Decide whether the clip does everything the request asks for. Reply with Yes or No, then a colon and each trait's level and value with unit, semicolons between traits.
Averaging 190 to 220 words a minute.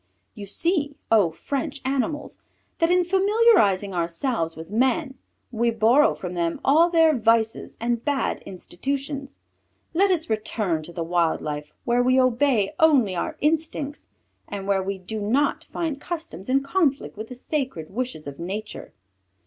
No: average, 150 wpm